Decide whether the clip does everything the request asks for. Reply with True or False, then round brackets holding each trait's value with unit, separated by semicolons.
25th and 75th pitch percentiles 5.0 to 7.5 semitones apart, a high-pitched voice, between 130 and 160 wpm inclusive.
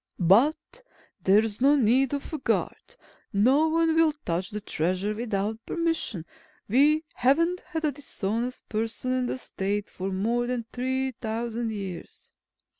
True (5.4 semitones; 240 Hz; 140 wpm)